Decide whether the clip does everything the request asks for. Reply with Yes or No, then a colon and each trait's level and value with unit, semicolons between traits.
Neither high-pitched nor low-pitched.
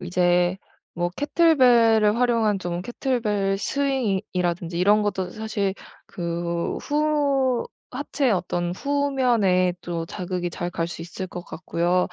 No: high, 195 Hz